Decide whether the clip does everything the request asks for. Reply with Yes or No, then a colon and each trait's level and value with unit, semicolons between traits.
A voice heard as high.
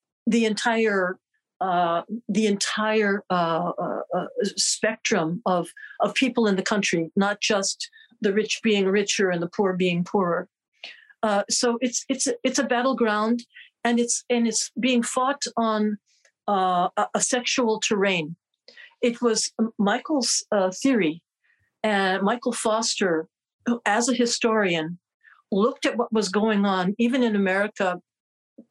Yes: high, 215 Hz